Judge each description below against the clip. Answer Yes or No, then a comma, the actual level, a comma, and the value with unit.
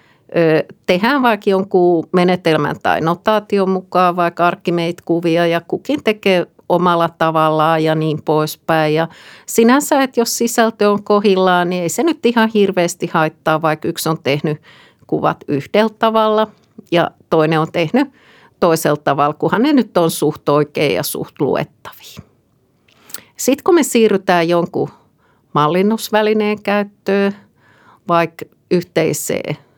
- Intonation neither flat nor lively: Yes, average, 4.9 semitones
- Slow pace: No, average, 125 wpm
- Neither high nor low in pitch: Yes, medium, 175 Hz